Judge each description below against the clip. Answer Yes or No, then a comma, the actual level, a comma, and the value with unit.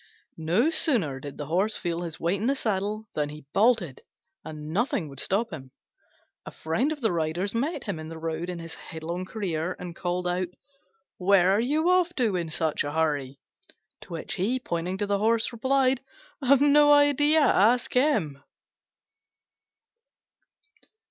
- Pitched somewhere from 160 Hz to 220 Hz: Yes, high, 190 Hz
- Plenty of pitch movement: Yes, wide, 7.2 semitones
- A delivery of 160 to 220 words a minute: Yes, average, 165 wpm